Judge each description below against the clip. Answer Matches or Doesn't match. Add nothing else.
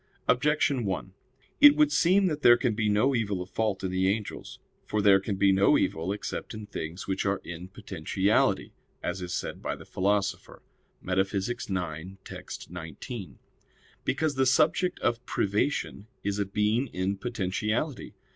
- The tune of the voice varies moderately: Matches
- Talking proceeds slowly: Doesn't match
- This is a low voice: Matches